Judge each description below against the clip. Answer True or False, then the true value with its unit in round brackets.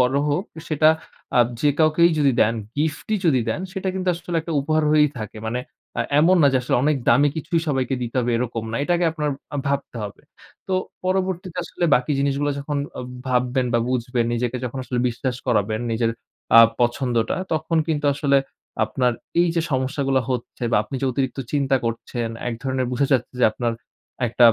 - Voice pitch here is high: False (135 Hz)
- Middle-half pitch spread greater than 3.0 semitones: True (4.1 semitones)